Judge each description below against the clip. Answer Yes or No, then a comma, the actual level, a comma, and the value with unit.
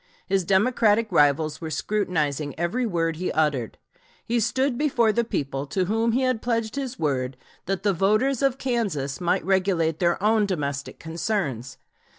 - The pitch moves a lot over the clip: Yes, wide, 6.7 semitones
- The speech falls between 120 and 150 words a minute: No, average, 160 wpm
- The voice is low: No, high, 190 Hz